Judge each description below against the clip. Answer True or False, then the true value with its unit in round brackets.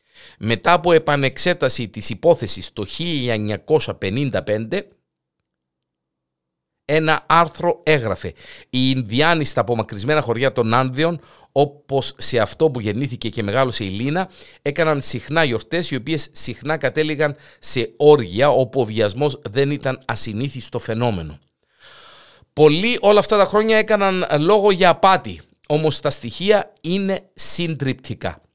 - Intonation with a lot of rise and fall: True (5.7 semitones)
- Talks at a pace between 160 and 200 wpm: False (120 wpm)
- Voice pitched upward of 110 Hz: True (135 Hz)